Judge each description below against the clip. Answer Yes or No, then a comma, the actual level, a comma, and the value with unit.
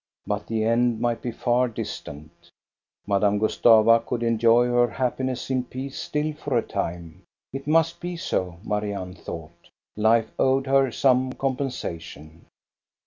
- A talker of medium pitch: No, low, 115 Hz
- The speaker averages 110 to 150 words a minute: Yes, average, 140 wpm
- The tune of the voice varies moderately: Yes, average, 4.2 semitones